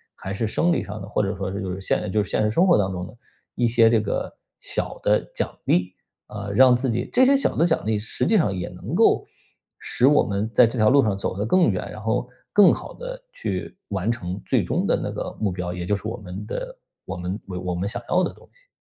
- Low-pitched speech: Yes, low, 105 Hz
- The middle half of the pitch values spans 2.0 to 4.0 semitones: No, average, 4.5 semitones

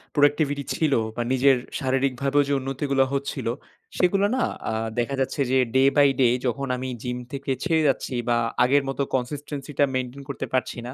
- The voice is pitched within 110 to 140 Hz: Yes, low, 135 Hz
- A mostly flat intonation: Yes, narrow, 1.7 semitones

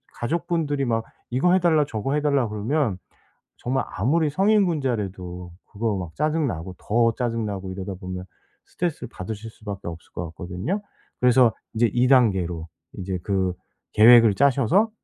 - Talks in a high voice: No, low, 115 Hz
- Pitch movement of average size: No, wide, 6.9 semitones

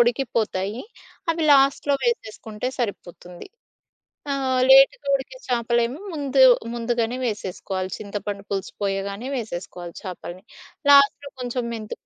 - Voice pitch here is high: Yes, high, 230 Hz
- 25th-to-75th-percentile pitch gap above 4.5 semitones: Yes, average, 5.1 semitones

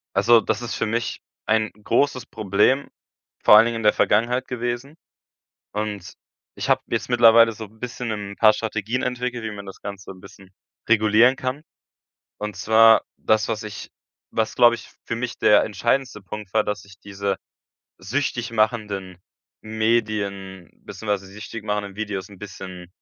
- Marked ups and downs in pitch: No, narrow, 2.6 semitones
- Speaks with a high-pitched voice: No, low, 110 Hz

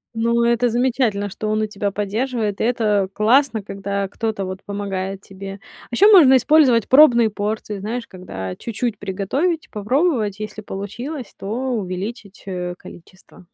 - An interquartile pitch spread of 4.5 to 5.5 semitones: No, average, 3.6 semitones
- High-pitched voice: Yes, high, 215 Hz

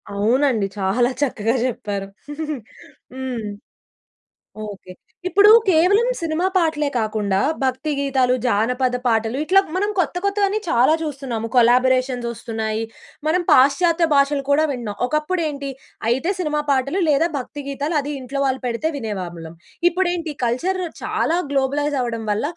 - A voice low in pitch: No, very high, 265 Hz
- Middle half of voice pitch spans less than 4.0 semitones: No, average, 5.1 semitones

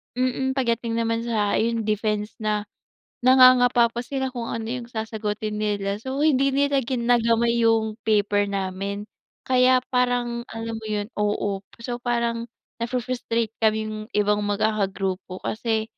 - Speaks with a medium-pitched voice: No, high, 230 Hz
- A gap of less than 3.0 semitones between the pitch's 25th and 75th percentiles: Yes, narrow, 2.6 semitones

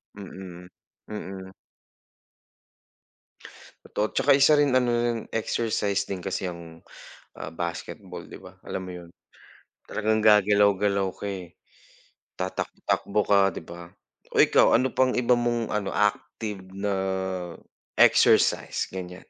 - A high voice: No, low, 100 Hz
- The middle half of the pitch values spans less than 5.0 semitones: Yes, average, 3.1 semitones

